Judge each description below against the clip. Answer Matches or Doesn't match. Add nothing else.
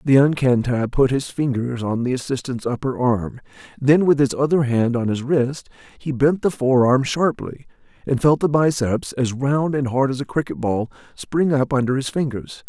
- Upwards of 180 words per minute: Matches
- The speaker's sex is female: Doesn't match